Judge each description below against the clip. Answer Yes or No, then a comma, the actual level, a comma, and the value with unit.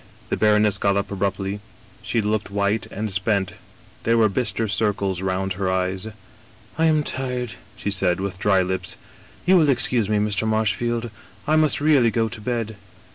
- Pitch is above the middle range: No, low, 105 Hz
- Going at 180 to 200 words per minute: Yes, average, 190 wpm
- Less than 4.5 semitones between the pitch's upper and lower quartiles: Yes, average, 3.1 semitones